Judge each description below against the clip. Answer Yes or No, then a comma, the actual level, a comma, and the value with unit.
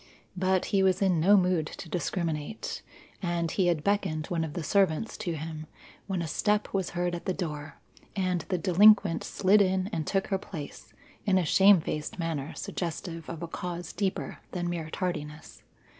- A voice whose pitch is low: No, medium, 175 Hz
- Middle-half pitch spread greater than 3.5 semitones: No, average, 2.9 semitones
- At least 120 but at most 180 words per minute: Yes, average, 175 wpm